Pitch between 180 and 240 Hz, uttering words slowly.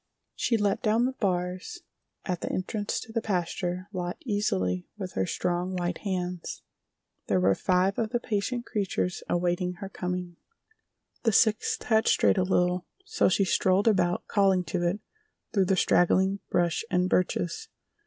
No: medium, 185 Hz; average, 155 wpm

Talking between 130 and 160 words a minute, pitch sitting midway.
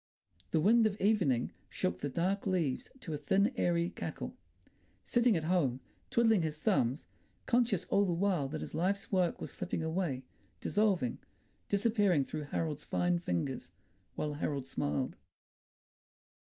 Yes: average, 140 wpm; medium, 175 Hz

